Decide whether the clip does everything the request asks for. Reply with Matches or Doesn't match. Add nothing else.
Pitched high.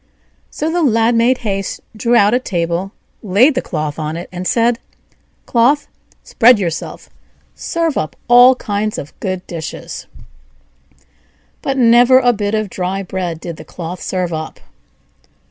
Matches